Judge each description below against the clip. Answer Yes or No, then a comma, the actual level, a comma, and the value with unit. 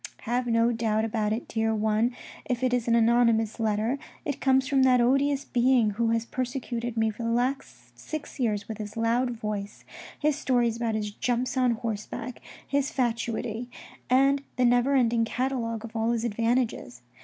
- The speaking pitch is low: No, high, 235 Hz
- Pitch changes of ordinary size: No, narrow, 2.3 semitones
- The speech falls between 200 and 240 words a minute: No, average, 180 wpm